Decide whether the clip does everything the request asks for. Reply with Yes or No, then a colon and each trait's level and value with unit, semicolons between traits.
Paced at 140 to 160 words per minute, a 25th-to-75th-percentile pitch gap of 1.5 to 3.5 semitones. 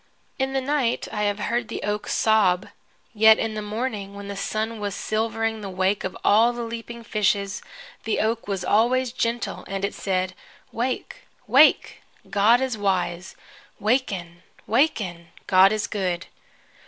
Yes: average, 155 wpm; average, 2.8 semitones